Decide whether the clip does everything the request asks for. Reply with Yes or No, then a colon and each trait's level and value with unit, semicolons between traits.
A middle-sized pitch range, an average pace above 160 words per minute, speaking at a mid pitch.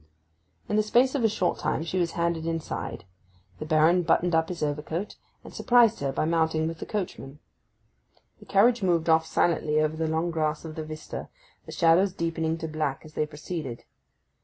No: narrow, 2.3 semitones; average, 185 wpm; medium, 165 Hz